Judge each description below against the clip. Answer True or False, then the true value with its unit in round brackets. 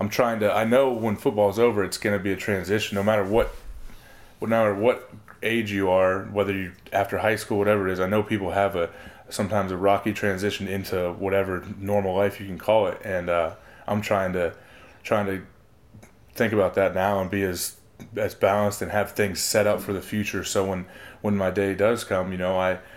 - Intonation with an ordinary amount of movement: False (2.0 semitones)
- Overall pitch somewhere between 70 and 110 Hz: True (100 Hz)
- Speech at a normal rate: False (215 wpm)